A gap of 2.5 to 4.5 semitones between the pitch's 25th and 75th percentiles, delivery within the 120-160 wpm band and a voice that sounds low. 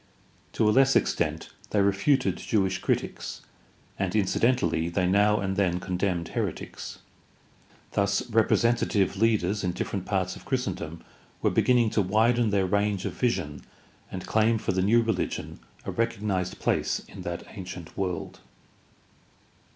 Yes: average, 3.3 semitones; average, 140 wpm; low, 100 Hz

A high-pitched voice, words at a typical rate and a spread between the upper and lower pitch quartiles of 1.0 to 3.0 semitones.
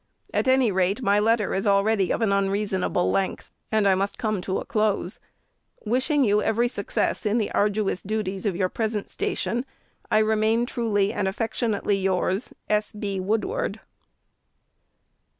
Yes: high, 210 Hz; average, 150 wpm; narrow, 2.4 semitones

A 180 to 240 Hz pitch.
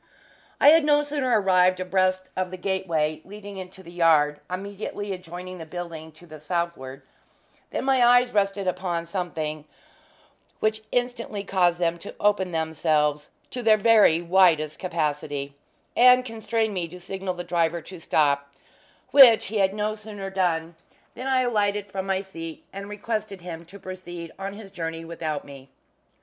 Yes: medium, 185 Hz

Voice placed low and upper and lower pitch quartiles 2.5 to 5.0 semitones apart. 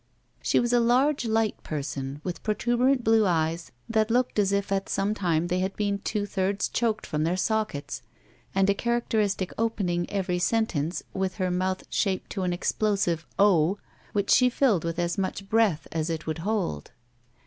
No: high, 195 Hz; average, 4.0 semitones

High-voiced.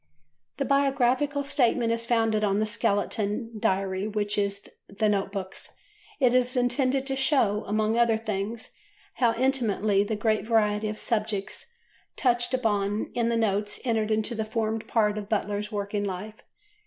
Yes: high, 220 Hz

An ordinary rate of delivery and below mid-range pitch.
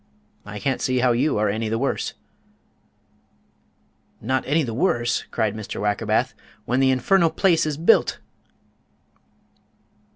No: slow, 130 wpm; low, 125 Hz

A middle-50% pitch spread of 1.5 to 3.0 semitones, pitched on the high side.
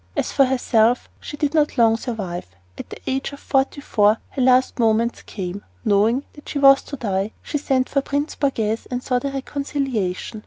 No: average, 4.1 semitones; very high, 250 Hz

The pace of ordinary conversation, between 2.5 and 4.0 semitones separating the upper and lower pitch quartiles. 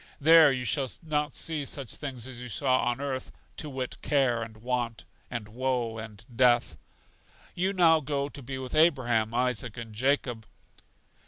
Yes: average, 165 wpm; average, 3.1 semitones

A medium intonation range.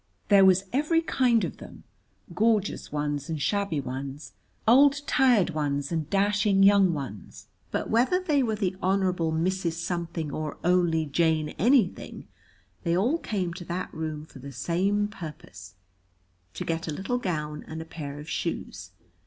Yes: average, 5.0 semitones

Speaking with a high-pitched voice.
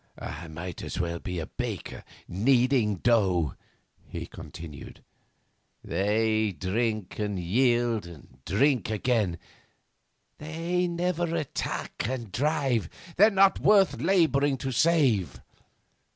No: low, 115 Hz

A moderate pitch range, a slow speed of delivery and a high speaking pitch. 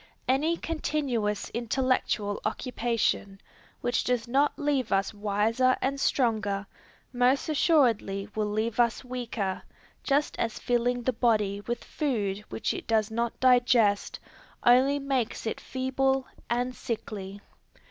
Yes: average, 3.4 semitones; slow, 120 wpm; high, 240 Hz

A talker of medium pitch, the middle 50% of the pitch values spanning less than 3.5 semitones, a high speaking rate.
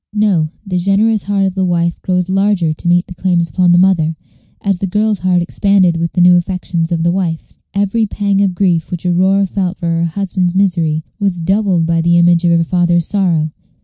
Yes: medium, 180 Hz; narrow, 2.4 semitones; fast, 210 wpm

